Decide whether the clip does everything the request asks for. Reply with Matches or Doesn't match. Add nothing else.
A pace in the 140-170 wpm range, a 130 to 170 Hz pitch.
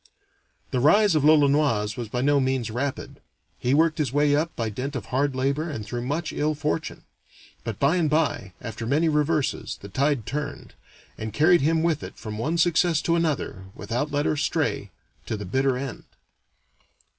Doesn't match